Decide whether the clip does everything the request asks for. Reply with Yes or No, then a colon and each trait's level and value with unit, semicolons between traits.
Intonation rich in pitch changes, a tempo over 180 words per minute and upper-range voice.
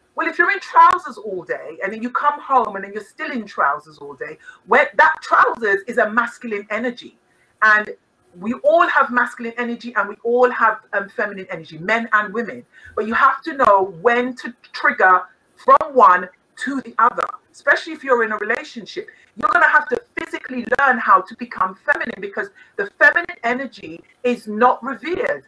Yes: wide, 5.9 semitones; average, 190 wpm; high, 245 Hz